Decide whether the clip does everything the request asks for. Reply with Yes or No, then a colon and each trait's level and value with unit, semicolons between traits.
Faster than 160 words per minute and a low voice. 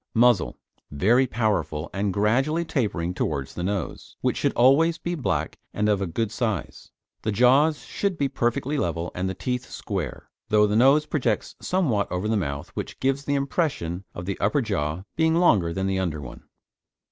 Yes: average, 180 wpm; low, 110 Hz